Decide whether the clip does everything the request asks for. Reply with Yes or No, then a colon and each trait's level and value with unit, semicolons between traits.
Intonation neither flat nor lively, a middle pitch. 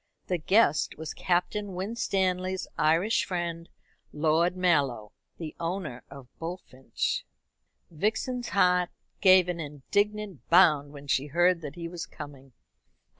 Yes: average, 3.7 semitones; medium, 175 Hz